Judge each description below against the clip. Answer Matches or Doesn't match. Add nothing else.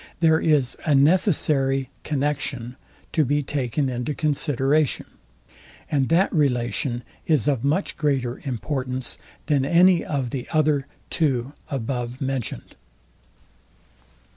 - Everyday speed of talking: Doesn't match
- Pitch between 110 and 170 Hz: Matches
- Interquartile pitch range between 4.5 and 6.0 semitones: Doesn't match